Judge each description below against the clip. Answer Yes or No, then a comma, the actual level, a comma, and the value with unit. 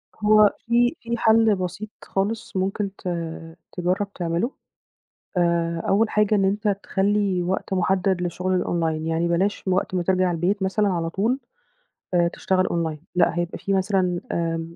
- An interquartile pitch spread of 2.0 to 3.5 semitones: Yes, average, 3.0 semitones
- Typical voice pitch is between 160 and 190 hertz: Yes, medium, 185 Hz